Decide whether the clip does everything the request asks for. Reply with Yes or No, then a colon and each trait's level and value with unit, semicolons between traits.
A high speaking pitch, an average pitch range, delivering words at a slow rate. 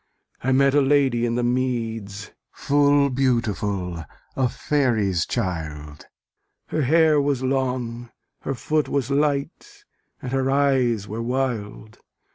No: low, 125 Hz; average, 3.8 semitones; slow, 120 wpm